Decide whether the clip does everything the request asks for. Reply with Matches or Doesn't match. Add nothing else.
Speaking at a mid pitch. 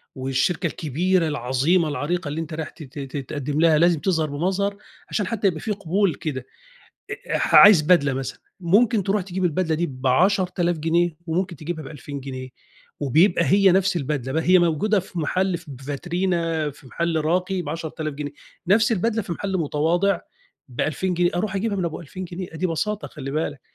Matches